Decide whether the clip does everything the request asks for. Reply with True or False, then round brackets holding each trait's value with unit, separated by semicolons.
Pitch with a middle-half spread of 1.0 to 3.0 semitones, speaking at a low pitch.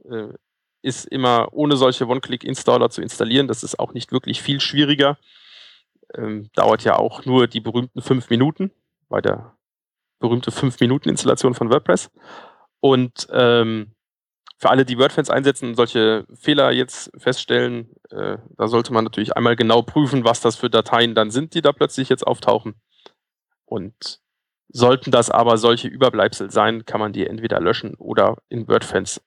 True (2.7 semitones; 120 Hz)